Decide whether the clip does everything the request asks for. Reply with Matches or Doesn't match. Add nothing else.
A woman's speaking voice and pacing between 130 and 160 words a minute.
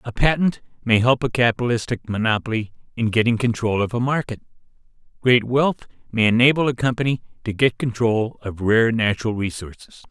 Doesn't match